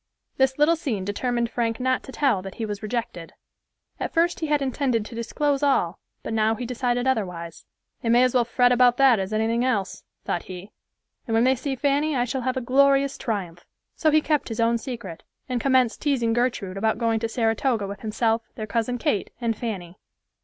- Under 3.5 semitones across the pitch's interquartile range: Yes, average, 3.1 semitones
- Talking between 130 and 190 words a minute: No, fast, 205 wpm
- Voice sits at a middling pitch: No, high, 235 Hz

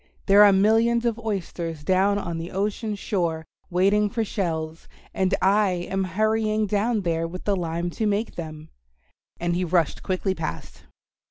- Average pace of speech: Yes, average, 160 wpm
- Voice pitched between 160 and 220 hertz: Yes, high, 190 Hz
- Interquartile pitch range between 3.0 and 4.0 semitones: Yes, average, 3.6 semitones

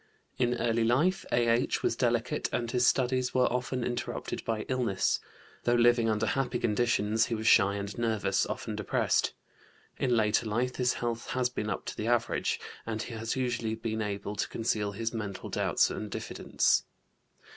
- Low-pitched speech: Yes, low, 115 Hz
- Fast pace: No, average, 170 wpm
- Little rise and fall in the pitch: Yes, narrow, 2.1 semitones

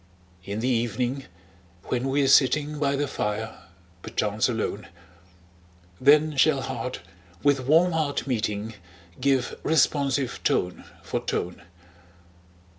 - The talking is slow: Yes, slow, 110 wpm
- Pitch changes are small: No, average, 4.0 semitones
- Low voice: Yes, low, 130 Hz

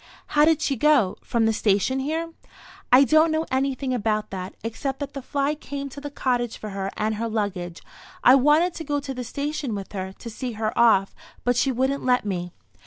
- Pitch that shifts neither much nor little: Yes, average, 4.8 semitones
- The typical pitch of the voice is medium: No, very high, 255 Hz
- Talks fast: Yes, fast, 210 wpm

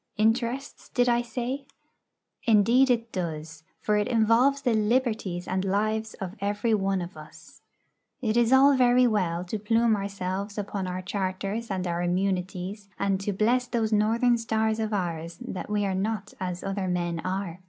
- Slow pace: No, average, 165 wpm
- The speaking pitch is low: No, high, 205 Hz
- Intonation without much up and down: No, average, 3.7 semitones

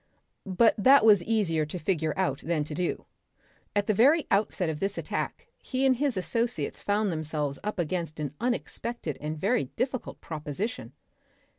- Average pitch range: No, wide, 6.7 semitones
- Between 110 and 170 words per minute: Yes, average, 160 wpm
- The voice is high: Yes, high, 195 Hz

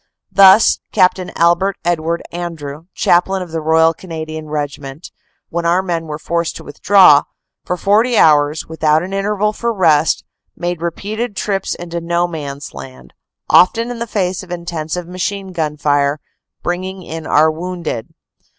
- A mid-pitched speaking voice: Yes, medium, 170 Hz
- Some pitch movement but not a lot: Yes, average, 3.3 semitones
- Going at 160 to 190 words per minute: No, average, 150 wpm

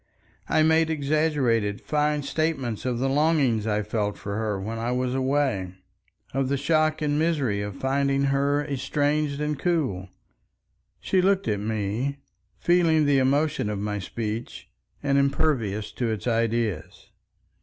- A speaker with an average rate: Yes, average, 145 wpm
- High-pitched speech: No, low, 135 Hz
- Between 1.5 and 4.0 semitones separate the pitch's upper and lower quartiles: No, wide, 5.4 semitones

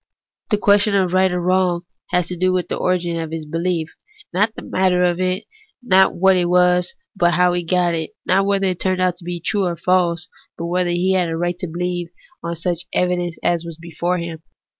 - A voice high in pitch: No, medium, 180 Hz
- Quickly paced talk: Yes, fast, 220 wpm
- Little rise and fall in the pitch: Yes, narrow, 1.3 semitones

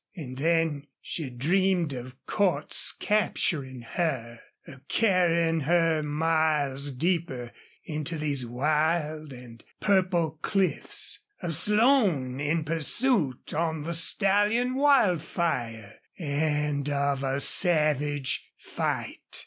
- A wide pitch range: No, average, 3.8 semitones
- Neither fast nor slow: No, slow, 100 wpm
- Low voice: No, medium, 155 Hz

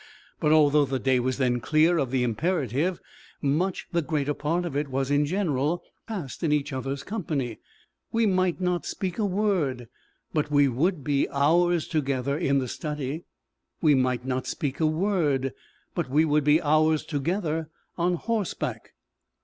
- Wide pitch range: No, average, 4.1 semitones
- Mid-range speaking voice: Yes, medium, 150 Hz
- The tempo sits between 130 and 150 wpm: No, average, 165 wpm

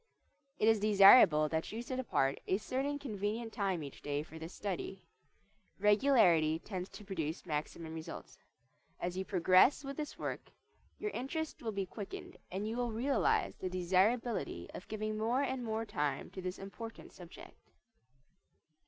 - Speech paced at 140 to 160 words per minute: Yes, average, 155 wpm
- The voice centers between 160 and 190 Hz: No, high, 205 Hz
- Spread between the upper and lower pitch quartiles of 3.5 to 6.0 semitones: Yes, average, 5.1 semitones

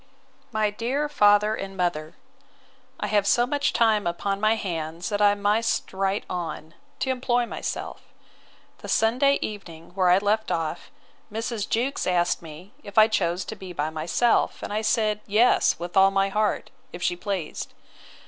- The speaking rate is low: No, average, 160 wpm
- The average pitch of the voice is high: Yes, high, 205 Hz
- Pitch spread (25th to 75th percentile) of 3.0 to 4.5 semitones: Yes, average, 3.7 semitones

